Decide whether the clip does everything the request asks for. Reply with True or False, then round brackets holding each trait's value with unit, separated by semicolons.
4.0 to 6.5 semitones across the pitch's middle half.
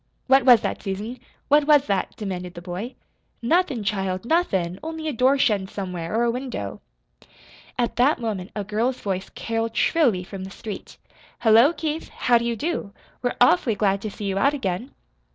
True (5.3 semitones)